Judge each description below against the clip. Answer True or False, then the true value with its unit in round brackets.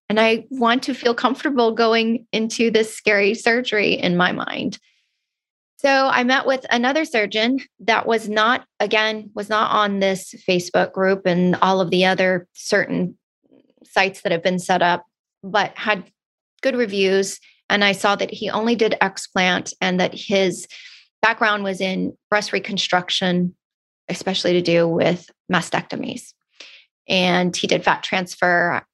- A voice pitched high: True (205 Hz)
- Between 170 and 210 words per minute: False (150 wpm)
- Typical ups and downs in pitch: True (3.6 semitones)